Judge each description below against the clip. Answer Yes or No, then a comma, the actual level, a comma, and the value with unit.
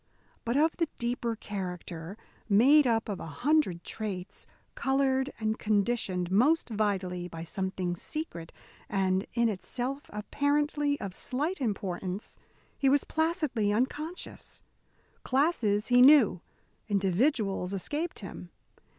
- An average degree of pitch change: No, wide, 6.7 semitones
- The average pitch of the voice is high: Yes, high, 220 Hz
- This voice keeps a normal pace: No, slow, 115 wpm